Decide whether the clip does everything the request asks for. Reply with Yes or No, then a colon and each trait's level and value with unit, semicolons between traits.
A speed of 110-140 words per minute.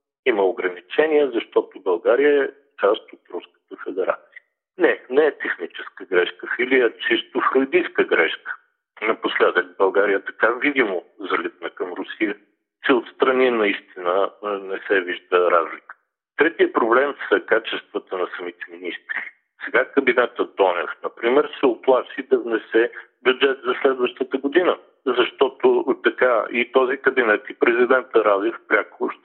Yes: average, 125 wpm